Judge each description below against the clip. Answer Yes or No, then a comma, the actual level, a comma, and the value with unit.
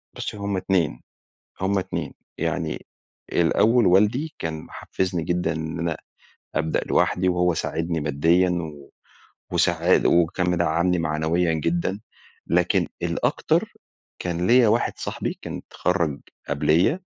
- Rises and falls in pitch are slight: Yes, narrow, 2.3 semitones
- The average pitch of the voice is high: No, very low, 85 Hz